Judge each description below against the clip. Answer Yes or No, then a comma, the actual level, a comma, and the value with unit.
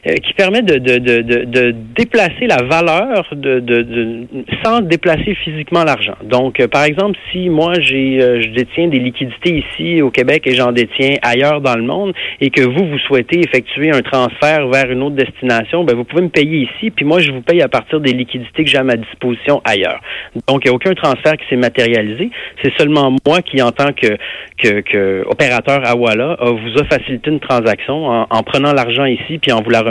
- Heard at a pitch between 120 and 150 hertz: Yes, low, 135 Hz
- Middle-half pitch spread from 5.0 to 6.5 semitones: No, average, 4.3 semitones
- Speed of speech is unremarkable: Yes, average, 210 wpm